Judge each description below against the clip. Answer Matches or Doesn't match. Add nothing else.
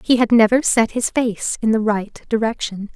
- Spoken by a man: Doesn't match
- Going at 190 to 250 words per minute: Matches